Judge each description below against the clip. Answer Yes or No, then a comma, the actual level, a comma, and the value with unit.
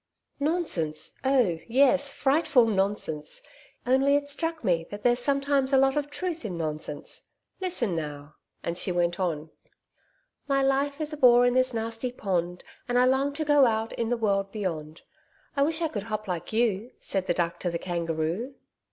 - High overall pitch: Yes, high, 235 Hz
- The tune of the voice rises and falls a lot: Yes, wide, 7.8 semitones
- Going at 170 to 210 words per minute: Yes, average, 180 wpm